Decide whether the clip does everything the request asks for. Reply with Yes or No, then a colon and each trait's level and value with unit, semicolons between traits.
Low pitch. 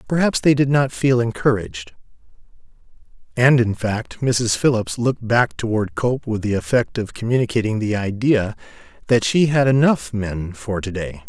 Yes: low, 115 Hz